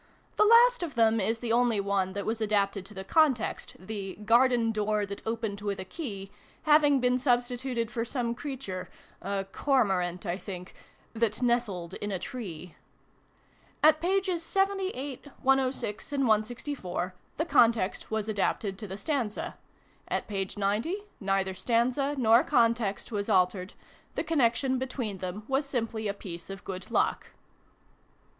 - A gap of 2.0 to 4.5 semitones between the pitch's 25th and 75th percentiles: No, average, 4.9 semitones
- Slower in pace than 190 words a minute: Yes, average, 155 wpm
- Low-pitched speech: No, high, 225 Hz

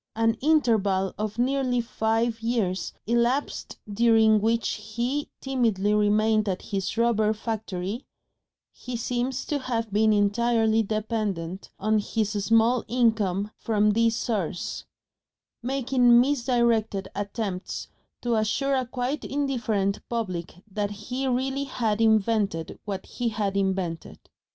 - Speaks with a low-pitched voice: No, high, 225 Hz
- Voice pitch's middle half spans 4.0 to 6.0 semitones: No, average, 2.8 semitones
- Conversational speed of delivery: No, slow, 115 wpm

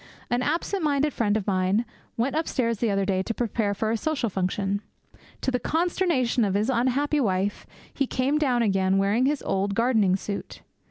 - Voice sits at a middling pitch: No, high, 230 Hz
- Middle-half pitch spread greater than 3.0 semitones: Yes, average, 5.2 semitones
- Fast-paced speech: No, average, 180 wpm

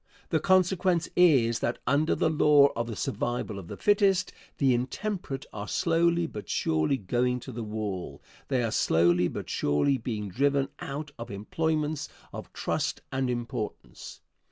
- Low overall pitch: Yes, low, 130 Hz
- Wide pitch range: Yes, wide, 6.5 semitones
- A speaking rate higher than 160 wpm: No, average, 155 wpm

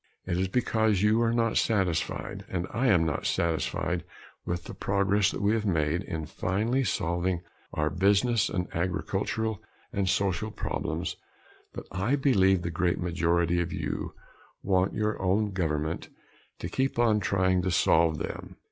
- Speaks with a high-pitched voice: No, very low, 95 Hz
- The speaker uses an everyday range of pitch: Yes, average, 3.7 semitones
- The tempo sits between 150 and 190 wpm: Yes, average, 155 wpm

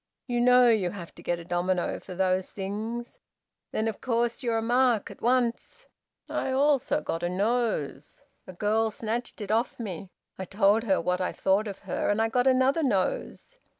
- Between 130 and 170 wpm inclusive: No, average, 185 wpm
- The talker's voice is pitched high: Yes, high, 220 Hz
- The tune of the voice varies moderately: Yes, average, 4.2 semitones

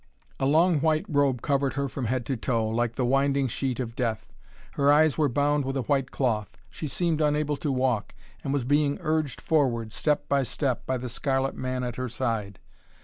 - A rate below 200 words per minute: No, fast, 205 wpm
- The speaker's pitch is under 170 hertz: Yes, low, 135 Hz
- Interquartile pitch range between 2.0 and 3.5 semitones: Yes, average, 2.9 semitones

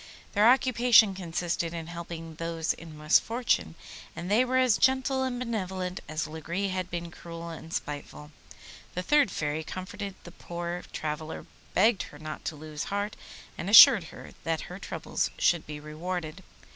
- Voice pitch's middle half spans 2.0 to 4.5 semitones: Yes, average, 4.2 semitones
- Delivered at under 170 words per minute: Yes, average, 160 wpm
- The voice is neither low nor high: Yes, medium, 175 Hz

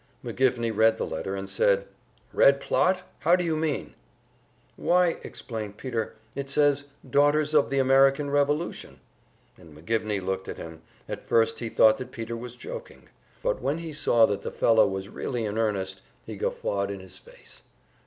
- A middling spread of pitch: No, wide, 5.9 semitones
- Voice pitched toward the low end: Yes, low, 115 Hz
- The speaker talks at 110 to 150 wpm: No, average, 170 wpm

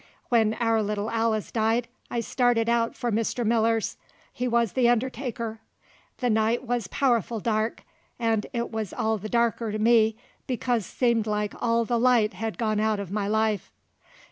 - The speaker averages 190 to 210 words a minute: No, average, 170 wpm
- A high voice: Yes, high, 225 Hz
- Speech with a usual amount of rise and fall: No, narrow, 1.6 semitones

